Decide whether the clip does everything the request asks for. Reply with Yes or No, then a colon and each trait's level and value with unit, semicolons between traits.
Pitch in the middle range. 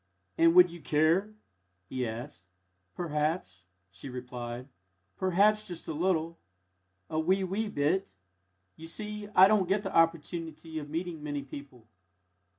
Yes: medium, 165 Hz